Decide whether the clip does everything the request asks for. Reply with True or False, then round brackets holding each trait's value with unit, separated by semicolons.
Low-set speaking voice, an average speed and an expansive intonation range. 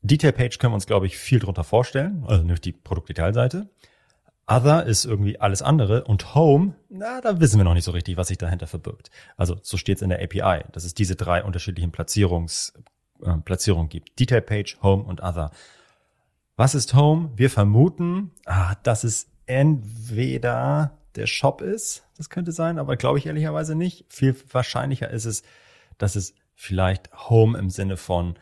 True (105 Hz; 175 wpm; 7.1 semitones)